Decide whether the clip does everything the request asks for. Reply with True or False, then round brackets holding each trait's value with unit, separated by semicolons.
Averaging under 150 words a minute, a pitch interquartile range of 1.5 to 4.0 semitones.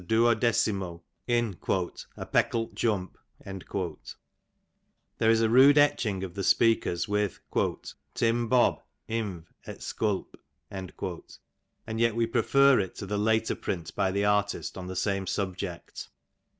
True (135 wpm; 3.3 semitones)